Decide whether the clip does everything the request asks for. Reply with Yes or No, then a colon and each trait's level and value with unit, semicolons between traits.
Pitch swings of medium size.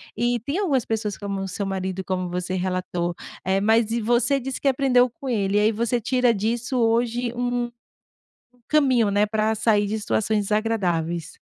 Yes: average, 3.9 semitones